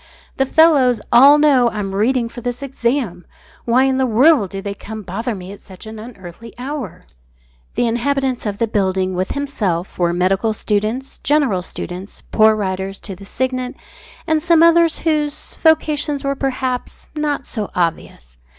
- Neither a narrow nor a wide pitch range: No, wide, 6.0 semitones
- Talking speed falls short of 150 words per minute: No, average, 165 wpm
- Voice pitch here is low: No, high, 235 Hz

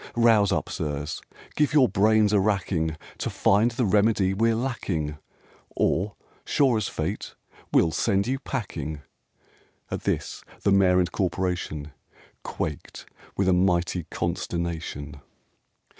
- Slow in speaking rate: Yes, slow, 125 wpm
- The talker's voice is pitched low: Yes, very low, 95 Hz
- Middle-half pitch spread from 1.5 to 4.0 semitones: No, average, 4.7 semitones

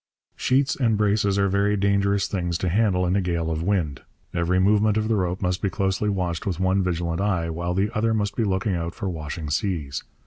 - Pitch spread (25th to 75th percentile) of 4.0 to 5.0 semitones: No, average, 2.9 semitones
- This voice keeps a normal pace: No, fast, 215 wpm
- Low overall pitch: Yes, very low, 95 Hz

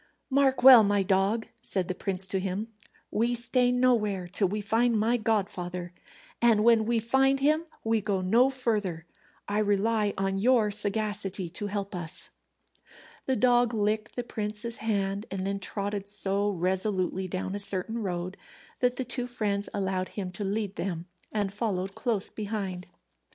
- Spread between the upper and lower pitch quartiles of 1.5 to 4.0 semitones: Yes, average, 3.0 semitones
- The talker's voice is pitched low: No, high, 205 Hz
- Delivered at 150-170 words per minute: Yes, average, 160 wpm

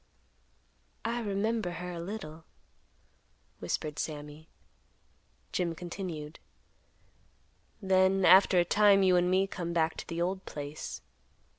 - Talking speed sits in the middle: No, slow, 115 wpm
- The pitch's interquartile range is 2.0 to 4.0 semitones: Yes, average, 2.9 semitones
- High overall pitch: No, medium, 180 Hz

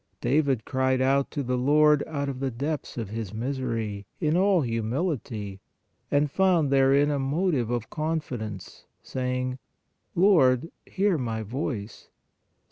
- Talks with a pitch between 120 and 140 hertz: Yes, low, 135 Hz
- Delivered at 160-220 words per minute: No, slow, 135 wpm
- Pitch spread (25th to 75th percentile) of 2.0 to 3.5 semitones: No, average, 4.3 semitones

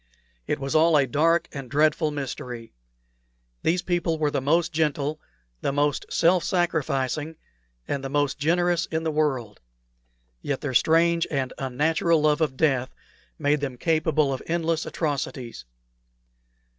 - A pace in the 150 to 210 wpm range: No, average, 140 wpm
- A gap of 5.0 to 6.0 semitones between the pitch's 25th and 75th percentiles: No, average, 3.0 semitones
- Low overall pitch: No, medium, 150 Hz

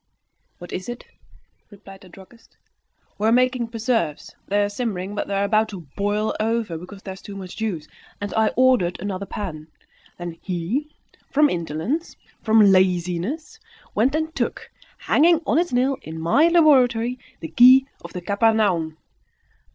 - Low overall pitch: No, high, 210 Hz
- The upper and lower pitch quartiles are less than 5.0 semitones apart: No, average, 5.3 semitones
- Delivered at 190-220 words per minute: No, average, 160 wpm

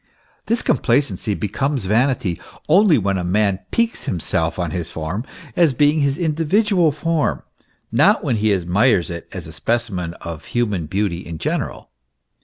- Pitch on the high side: No, low, 105 Hz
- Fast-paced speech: No, average, 150 wpm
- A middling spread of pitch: No, wide, 8.6 semitones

